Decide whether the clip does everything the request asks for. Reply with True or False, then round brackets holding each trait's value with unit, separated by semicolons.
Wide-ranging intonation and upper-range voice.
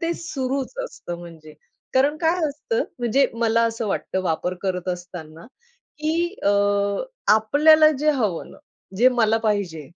True (8.8 semitones; 230 Hz)